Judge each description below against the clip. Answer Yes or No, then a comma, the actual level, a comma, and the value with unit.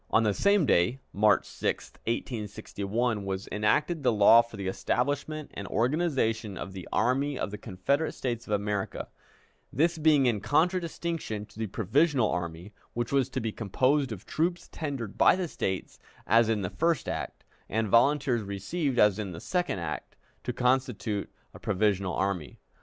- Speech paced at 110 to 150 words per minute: No, average, 165 wpm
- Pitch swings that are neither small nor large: No, wide, 5.9 semitones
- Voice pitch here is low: Yes, low, 115 Hz